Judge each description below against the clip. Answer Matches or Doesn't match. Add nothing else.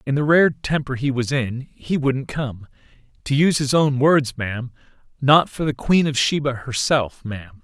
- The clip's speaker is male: Matches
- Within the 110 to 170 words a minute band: Doesn't match